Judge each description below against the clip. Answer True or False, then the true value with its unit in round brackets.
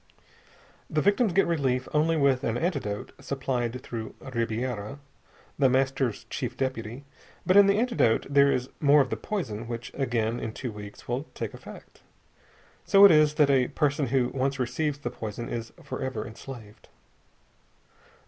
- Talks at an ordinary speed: True (160 wpm)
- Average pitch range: True (4.0 semitones)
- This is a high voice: False (130 Hz)